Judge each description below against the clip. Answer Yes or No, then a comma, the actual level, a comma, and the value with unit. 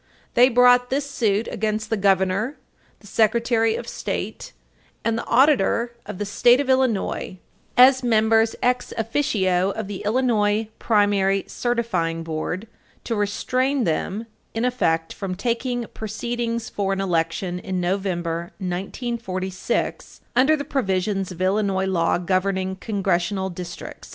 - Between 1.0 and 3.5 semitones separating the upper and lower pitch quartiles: No, average, 4.1 semitones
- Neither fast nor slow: No, slow, 130 wpm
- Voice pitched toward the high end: Yes, high, 210 Hz